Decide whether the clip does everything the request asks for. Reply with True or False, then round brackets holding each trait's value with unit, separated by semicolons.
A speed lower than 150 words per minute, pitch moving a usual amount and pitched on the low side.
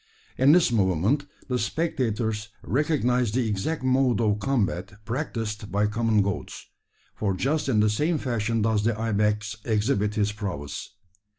True (140 wpm; 3.5 semitones; 110 Hz)